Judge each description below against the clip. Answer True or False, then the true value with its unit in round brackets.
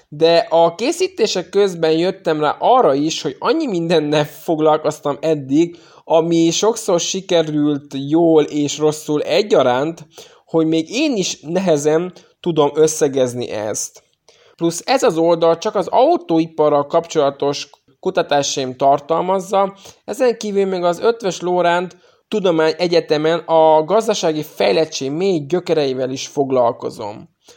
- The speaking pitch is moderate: True (165 Hz)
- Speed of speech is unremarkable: True (115 wpm)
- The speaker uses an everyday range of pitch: True (3.0 semitones)